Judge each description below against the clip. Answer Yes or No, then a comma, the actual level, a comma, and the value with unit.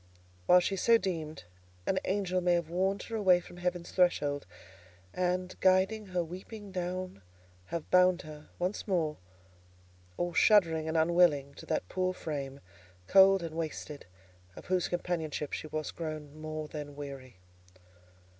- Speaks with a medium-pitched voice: Yes, medium, 175 Hz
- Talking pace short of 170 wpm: Yes, average, 145 wpm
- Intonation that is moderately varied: Yes, average, 3.0 semitones